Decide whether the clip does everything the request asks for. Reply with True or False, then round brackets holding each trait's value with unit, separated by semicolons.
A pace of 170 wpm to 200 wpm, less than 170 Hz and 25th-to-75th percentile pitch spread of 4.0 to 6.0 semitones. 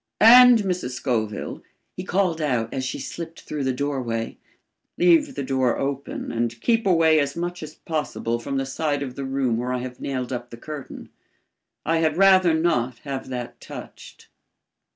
True (175 wpm; 140 Hz; 4.7 semitones)